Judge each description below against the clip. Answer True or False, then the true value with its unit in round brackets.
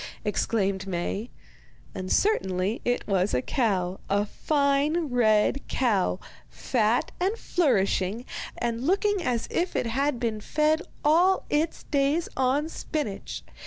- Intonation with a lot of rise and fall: True (7.0 semitones)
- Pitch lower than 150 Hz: False (245 Hz)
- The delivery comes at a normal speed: False (125 wpm)